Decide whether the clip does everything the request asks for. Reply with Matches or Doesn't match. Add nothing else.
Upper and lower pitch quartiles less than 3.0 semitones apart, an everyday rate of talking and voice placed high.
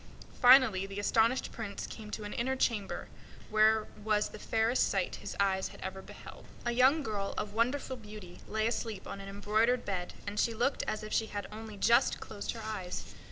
Matches